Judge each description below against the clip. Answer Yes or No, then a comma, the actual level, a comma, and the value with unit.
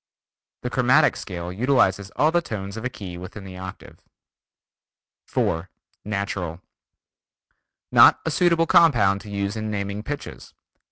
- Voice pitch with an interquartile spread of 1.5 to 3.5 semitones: No, average, 4.6 semitones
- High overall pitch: No, low, 100 Hz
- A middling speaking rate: No, slow, 130 wpm